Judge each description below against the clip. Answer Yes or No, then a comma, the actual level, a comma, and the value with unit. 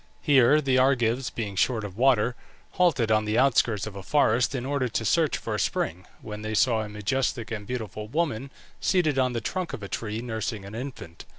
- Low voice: Yes, low, 115 Hz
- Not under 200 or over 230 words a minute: Yes, fast, 205 wpm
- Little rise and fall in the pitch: No, average, 3.9 semitones